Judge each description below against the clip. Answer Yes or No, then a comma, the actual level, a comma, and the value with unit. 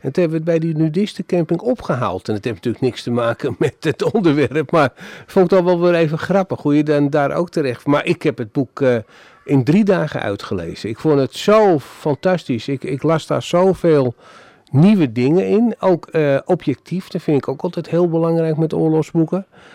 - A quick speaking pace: Yes, fast, 205 wpm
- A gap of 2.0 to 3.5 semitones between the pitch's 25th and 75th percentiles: No, average, 4.8 semitones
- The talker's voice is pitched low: No, medium, 155 Hz